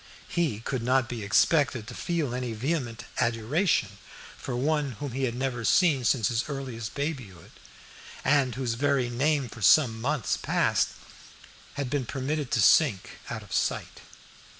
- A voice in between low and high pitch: No, low, 130 Hz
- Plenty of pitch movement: No, average, 3.6 semitones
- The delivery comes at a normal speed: Yes, average, 150 wpm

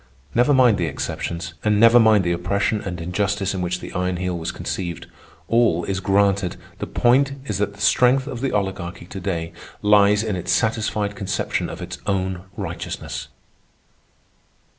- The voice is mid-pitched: No, low, 100 Hz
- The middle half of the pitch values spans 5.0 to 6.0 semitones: No, average, 3.3 semitones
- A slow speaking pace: No, average, 160 wpm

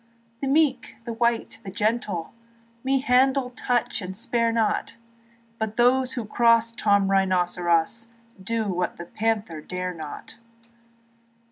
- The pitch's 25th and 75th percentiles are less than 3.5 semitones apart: No, average, 4.4 semitones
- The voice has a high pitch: Yes, high, 225 Hz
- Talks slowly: Yes, slow, 125 wpm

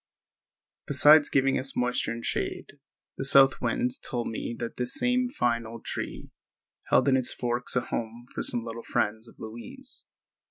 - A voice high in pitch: No, low, 125 Hz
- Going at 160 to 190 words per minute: Yes, average, 165 wpm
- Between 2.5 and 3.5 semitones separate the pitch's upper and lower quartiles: Yes, average, 2.8 semitones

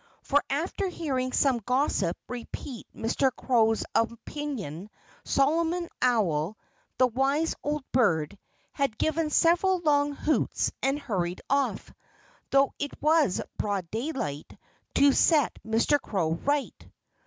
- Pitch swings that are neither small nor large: Yes, average, 5.0 semitones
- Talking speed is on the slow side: Yes, slow, 115 wpm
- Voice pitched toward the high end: Yes, very high, 270 Hz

